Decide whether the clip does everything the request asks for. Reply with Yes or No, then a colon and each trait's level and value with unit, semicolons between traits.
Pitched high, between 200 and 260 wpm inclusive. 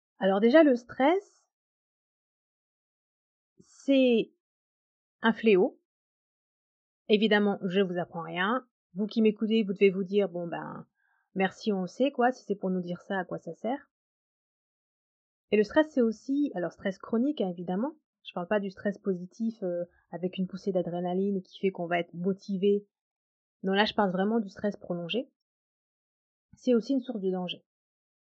No: high, 205 Hz; average, 165 wpm